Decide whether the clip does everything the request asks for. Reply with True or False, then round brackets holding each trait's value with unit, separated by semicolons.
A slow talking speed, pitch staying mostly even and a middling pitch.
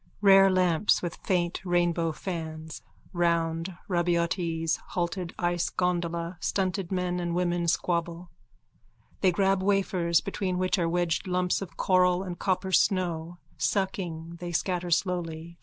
True (125 wpm; 1.6 semitones; 175 Hz)